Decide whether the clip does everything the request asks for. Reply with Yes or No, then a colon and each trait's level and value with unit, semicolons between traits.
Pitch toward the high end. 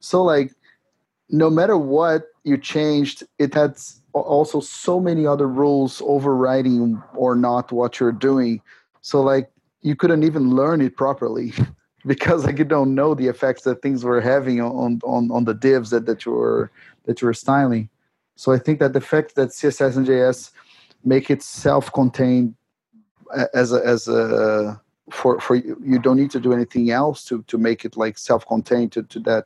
No: low, 130 Hz